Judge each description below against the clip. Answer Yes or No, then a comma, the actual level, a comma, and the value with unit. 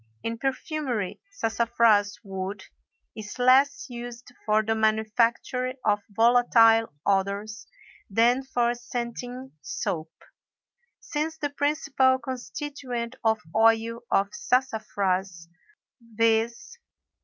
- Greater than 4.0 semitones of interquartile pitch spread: No, average, 2.9 semitones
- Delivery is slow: Yes, slow, 90 wpm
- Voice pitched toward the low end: No, high, 230 Hz